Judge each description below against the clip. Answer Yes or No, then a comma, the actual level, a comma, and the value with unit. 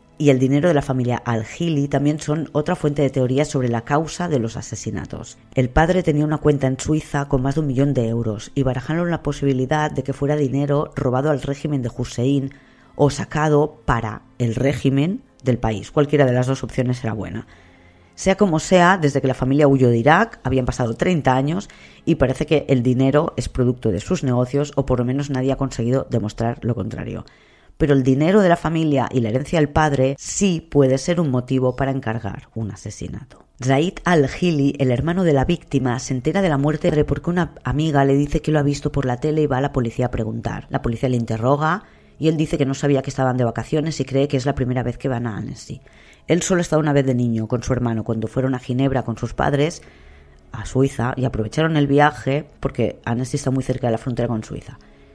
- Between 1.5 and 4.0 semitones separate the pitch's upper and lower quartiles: Yes, average, 3.3 semitones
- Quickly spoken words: Yes, fast, 225 wpm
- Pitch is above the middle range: No, low, 135 Hz